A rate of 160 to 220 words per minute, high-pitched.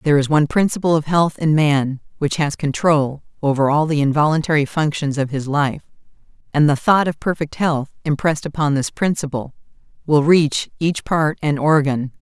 No: average, 170 wpm; medium, 150 Hz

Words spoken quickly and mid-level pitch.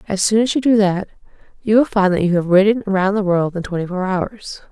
No: fast, 255 wpm; high, 200 Hz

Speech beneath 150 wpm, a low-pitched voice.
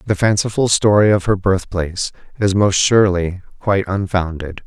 Yes: average, 140 wpm; very low, 95 Hz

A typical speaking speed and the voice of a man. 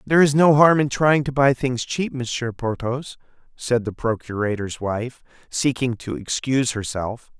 Yes: average, 160 wpm; male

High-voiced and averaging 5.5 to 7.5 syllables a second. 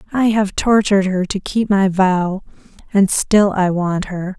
No: high, 195 Hz; 4.1 syllables/s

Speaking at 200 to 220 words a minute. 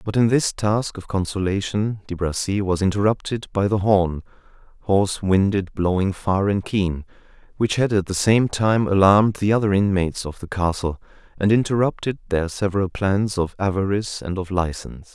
No: average, 165 wpm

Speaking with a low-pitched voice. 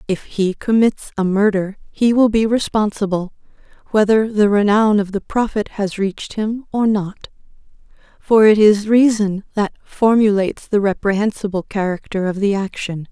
No: high, 205 Hz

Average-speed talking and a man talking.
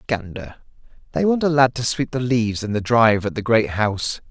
No: fast, 225 wpm; male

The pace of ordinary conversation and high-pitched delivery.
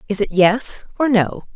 Yes: average, 190 wpm; high, 215 Hz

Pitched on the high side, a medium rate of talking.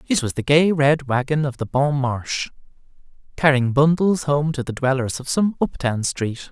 No: medium, 140 Hz; average, 195 wpm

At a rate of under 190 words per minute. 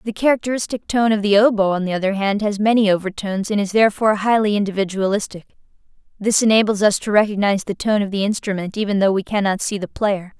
No: average, 200 wpm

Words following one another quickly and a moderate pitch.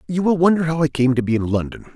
Yes: fast, 305 wpm; medium, 145 Hz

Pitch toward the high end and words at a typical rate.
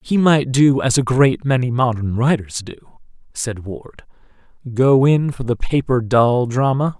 No: low, 125 Hz; average, 165 wpm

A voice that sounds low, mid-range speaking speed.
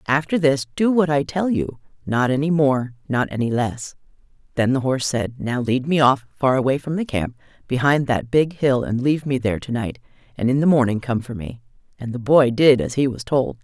No: low, 130 Hz; fast, 225 wpm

